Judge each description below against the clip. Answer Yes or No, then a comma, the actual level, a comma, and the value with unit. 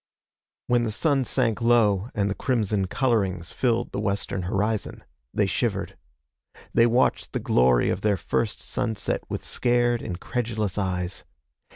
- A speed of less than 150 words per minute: Yes, average, 140 wpm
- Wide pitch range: No, average, 3.6 semitones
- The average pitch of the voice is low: Yes, low, 110 Hz